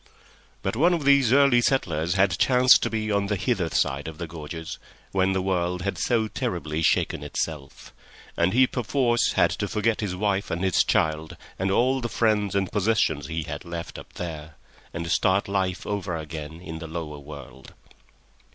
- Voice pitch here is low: Yes, very low, 95 Hz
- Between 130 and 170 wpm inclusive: No, average, 180 wpm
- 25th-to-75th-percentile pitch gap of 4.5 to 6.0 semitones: Yes, average, 5.1 semitones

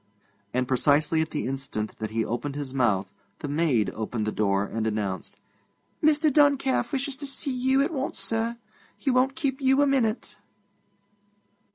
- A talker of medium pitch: Yes, medium, 160 Hz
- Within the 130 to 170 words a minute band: Yes, average, 165 wpm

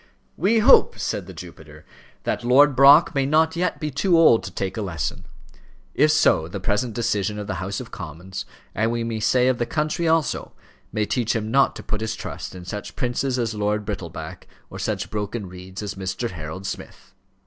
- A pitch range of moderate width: No, wide, 5.9 semitones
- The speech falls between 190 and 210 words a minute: Yes, average, 200 wpm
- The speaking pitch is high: No, low, 110 Hz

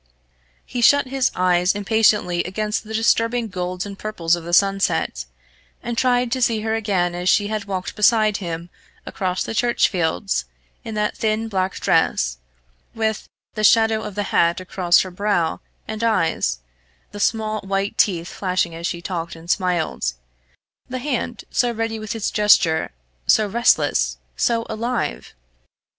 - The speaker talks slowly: No, average, 155 wpm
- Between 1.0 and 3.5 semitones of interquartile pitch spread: No, average, 3.9 semitones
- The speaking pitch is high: Yes, high, 205 Hz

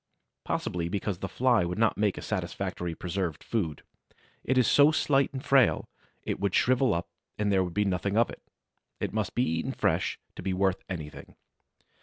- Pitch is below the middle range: Yes, low, 100 Hz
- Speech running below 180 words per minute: No, average, 185 wpm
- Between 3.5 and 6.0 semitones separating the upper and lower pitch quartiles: Yes, average, 5.1 semitones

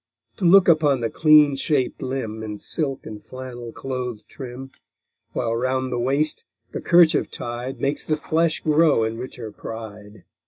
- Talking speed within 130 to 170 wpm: Yes, average, 155 wpm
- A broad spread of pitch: No, average, 4.6 semitones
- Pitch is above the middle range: No, low, 130 Hz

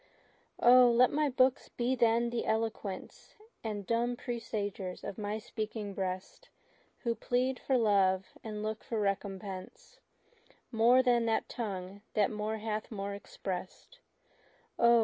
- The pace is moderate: No, slow, 130 wpm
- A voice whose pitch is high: Yes, high, 220 Hz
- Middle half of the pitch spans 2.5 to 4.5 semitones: Yes, average, 3.0 semitones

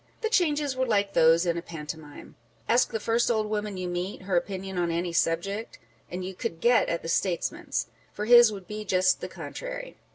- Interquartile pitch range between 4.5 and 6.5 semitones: Yes, average, 4.8 semitones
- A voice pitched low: No, high, 195 Hz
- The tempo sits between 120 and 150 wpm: No, average, 200 wpm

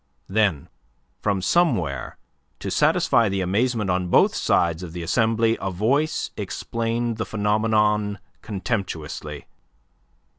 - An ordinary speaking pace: No, slow, 110 wpm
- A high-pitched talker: No, low, 105 Hz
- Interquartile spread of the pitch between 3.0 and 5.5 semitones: Yes, average, 3.6 semitones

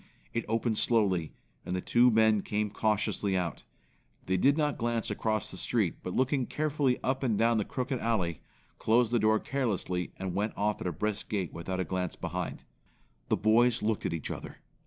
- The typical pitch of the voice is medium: No, low, 110 Hz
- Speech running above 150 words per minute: Yes, average, 190 wpm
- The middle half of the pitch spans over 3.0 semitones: Yes, average, 4.2 semitones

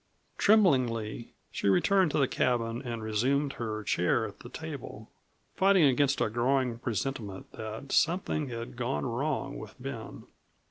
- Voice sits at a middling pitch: No, low, 125 Hz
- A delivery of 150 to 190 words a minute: No, average, 140 wpm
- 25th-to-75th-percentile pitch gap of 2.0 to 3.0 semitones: No, average, 3.6 semitones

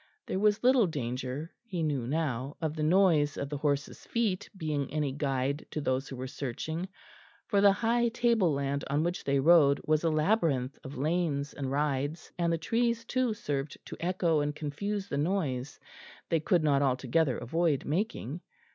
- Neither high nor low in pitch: Yes, medium, 155 Hz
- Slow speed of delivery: No, average, 175 wpm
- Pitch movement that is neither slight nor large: Yes, average, 4.6 semitones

